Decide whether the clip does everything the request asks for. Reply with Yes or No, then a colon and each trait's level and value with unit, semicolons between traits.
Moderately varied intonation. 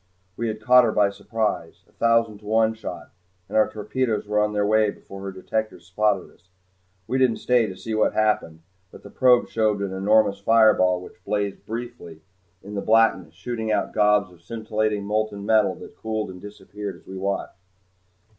No: narrow, 2.0 semitones